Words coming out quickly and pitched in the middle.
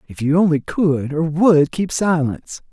No: average, 175 wpm; medium, 160 Hz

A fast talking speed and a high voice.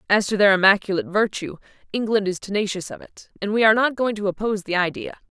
Yes: fast, 215 wpm; high, 200 Hz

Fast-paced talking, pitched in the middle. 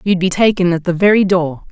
Yes: fast, 245 wpm; medium, 180 Hz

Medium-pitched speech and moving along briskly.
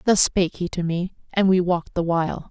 Yes: medium, 180 Hz; fast, 240 wpm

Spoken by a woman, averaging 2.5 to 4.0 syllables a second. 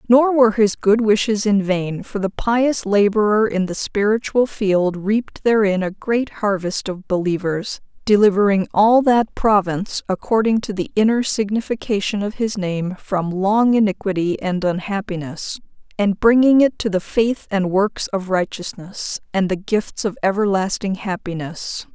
Yes: female; 3.9 syllables/s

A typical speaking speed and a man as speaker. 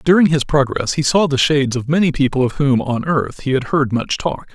No: fast, 250 wpm; male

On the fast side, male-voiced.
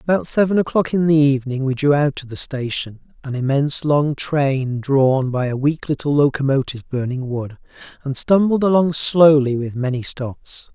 No: average, 175 wpm; male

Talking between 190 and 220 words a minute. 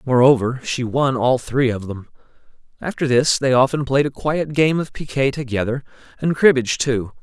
No: average, 175 wpm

